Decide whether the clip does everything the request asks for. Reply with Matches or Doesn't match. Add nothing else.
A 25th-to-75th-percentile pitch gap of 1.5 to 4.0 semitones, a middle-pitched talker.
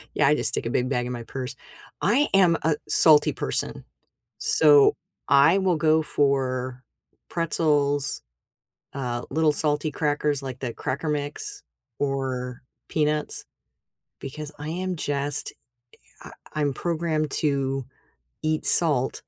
Matches